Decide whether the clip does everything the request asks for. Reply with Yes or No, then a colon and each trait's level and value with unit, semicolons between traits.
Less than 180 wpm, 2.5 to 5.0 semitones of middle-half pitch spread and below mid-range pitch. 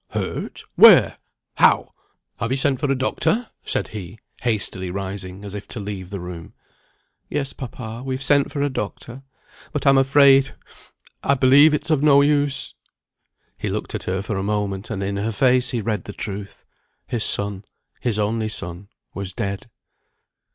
No: average, 165 wpm; wide, 5.4 semitones; low, 110 Hz